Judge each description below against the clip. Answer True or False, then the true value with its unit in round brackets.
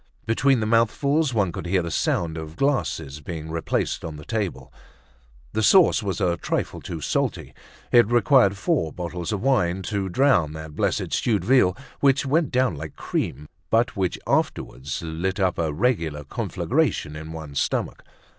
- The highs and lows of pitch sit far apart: True (7.1 semitones)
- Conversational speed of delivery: True (165 wpm)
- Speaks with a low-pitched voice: True (95 Hz)